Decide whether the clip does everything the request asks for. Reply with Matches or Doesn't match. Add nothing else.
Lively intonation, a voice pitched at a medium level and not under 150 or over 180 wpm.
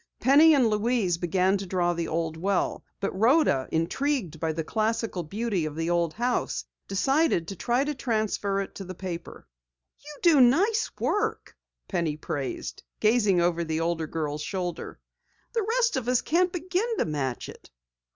Doesn't match